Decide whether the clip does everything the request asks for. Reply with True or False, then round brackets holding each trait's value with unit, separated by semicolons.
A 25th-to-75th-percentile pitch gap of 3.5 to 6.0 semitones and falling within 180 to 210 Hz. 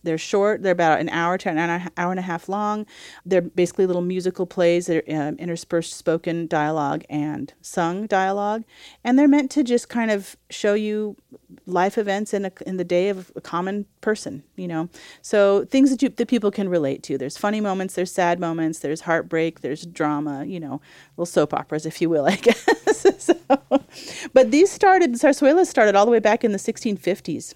True (4.7 semitones; 185 Hz)